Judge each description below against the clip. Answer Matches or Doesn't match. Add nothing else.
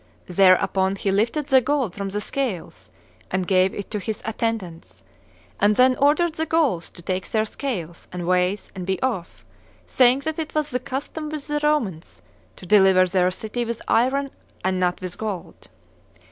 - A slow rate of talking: Doesn't match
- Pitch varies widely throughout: Matches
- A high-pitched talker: Matches